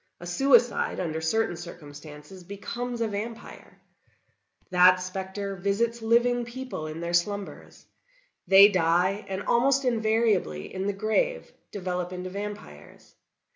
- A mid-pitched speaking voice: No, high, 195 Hz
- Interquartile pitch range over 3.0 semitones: Yes, average, 4.5 semitones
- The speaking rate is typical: No, slow, 120 wpm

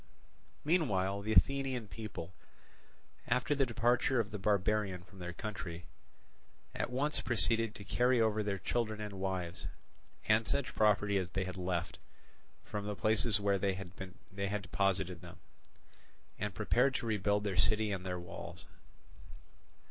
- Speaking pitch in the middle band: No, low, 105 Hz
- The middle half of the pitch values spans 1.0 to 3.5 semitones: Yes, average, 3.0 semitones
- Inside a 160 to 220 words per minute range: No, average, 140 wpm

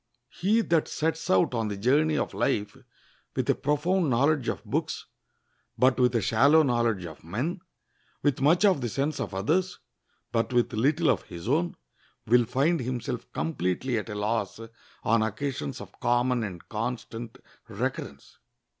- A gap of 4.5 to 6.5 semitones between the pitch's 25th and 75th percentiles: Yes, average, 5.2 semitones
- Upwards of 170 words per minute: No, average, 155 wpm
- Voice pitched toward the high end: No, low, 125 Hz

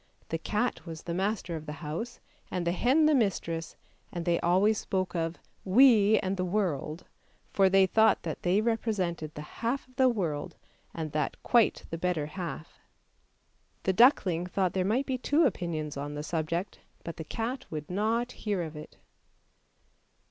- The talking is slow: No, average, 170 wpm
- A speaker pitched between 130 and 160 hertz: No, medium, 185 Hz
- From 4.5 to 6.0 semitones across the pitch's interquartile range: Yes, average, 5.1 semitones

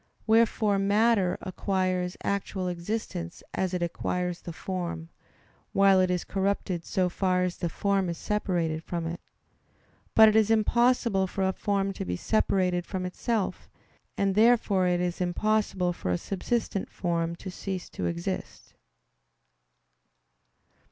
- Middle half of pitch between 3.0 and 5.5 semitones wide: No, narrow, 2.4 semitones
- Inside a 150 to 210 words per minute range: No, average, 140 wpm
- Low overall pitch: No, medium, 185 Hz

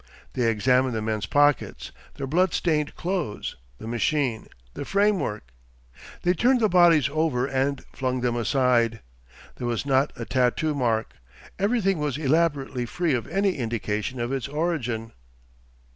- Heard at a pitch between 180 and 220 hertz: No, low, 135 Hz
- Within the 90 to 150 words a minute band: Yes, average, 140 wpm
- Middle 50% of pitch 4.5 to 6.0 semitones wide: Yes, average, 5.2 semitones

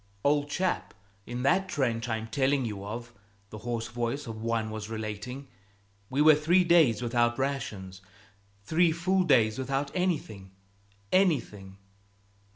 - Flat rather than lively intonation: No, average, 5.1 semitones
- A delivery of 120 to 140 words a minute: Yes, slow, 135 wpm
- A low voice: Yes, low, 125 Hz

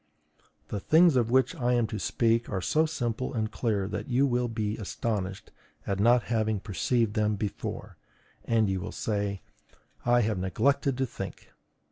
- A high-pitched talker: No, low, 115 Hz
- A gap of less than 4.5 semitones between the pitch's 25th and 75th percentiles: Yes, average, 3.1 semitones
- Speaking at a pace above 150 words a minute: Yes, average, 165 wpm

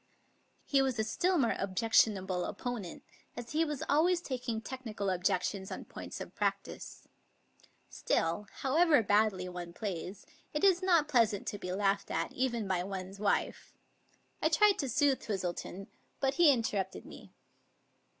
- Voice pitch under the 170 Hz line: No, high, 220 Hz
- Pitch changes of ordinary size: No, wide, 6.2 semitones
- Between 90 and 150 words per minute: Yes, average, 145 wpm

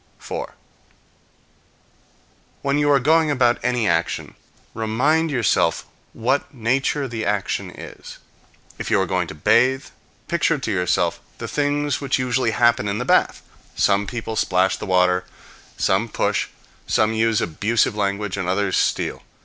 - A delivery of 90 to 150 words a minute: Yes, average, 140 wpm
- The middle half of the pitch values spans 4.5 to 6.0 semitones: Yes, average, 5.1 semitones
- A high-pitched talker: No, low, 115 Hz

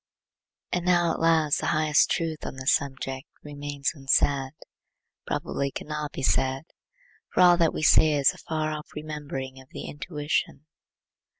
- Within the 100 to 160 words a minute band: Yes, average, 155 wpm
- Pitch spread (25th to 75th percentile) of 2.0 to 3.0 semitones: Yes, narrow, 2.4 semitones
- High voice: No, medium, 150 Hz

